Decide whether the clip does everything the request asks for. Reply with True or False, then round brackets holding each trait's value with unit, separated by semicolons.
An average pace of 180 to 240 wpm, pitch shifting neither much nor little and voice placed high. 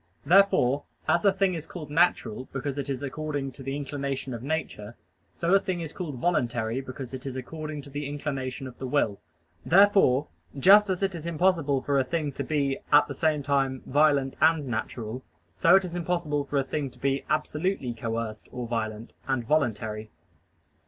False (185 wpm; 3.6 semitones; 140 Hz)